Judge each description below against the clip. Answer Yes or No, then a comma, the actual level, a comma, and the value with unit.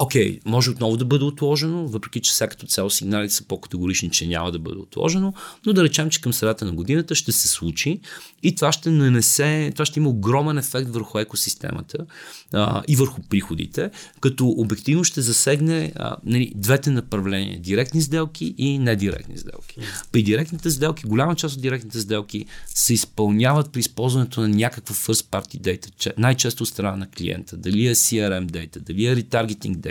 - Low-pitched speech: Yes, low, 120 Hz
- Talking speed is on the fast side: Yes, fast, 180 wpm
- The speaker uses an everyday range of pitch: No, wide, 5.7 semitones